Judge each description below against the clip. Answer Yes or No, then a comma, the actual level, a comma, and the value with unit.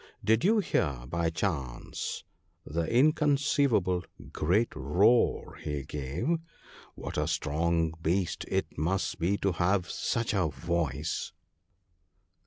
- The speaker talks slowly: Yes, slow, 110 wpm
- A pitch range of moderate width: No, wide, 5.9 semitones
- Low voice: Yes, very low, 85 Hz